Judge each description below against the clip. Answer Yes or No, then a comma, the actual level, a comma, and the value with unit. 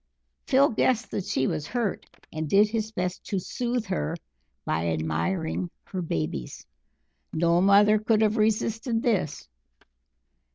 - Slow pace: Yes, slow, 130 wpm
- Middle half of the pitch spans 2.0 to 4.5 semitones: No, average, 5.2 semitones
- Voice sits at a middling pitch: No, high, 200 Hz